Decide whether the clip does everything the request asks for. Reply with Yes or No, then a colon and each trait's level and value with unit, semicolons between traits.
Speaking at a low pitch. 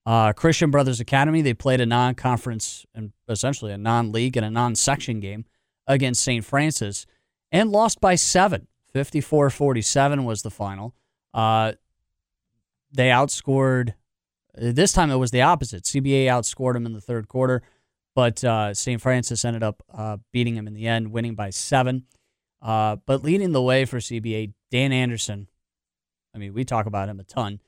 Yes: low, 120 Hz